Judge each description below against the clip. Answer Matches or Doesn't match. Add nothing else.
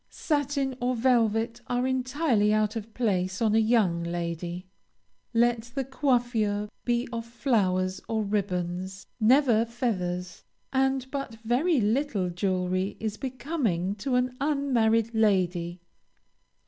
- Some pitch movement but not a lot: Matches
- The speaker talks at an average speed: Doesn't match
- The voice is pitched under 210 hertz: Doesn't match